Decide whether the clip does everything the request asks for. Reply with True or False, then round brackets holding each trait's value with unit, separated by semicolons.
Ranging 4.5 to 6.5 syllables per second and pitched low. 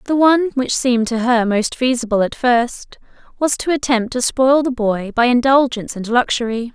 False (5.1 syllables/s; 245 Hz)